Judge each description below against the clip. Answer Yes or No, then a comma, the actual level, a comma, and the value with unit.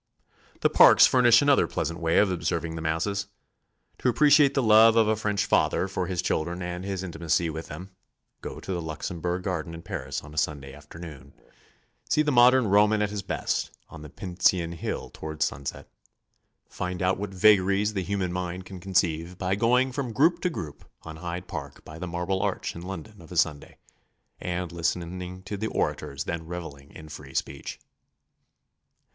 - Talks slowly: No, average, 180 wpm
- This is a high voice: No, very low, 90 Hz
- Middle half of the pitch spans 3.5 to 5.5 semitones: Yes, average, 3.8 semitones